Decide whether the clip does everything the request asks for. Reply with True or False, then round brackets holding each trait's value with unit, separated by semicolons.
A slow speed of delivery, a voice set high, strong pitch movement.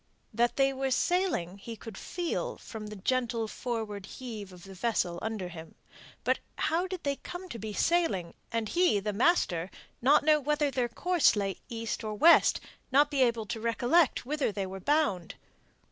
False (185 wpm; 235 Hz; 6.3 semitones)